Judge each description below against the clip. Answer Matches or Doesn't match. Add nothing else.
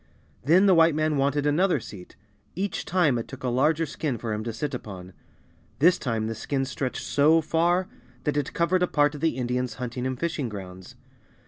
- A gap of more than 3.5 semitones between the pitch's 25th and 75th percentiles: Matches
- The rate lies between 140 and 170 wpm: Doesn't match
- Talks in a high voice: Doesn't match